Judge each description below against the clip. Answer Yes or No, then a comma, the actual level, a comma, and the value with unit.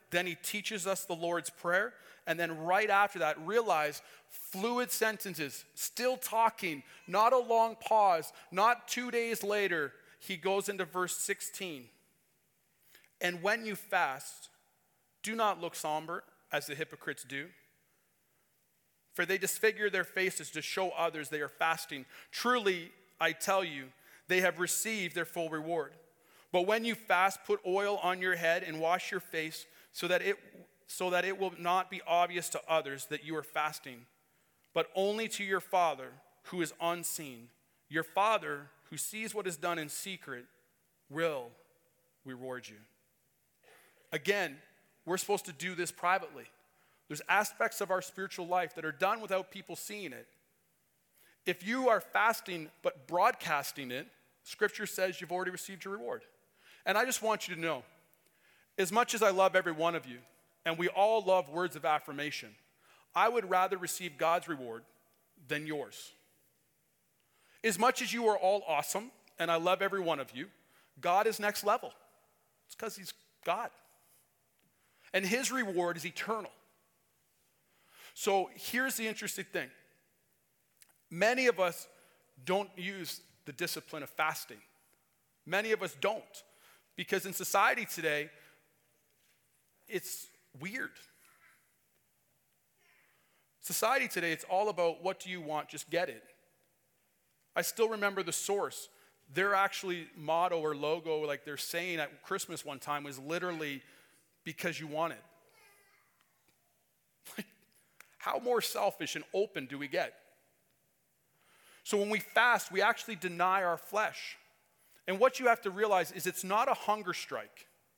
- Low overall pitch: No, medium, 180 Hz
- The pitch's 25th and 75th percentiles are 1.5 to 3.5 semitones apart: No, average, 4.2 semitones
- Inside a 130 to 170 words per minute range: Yes, average, 150 wpm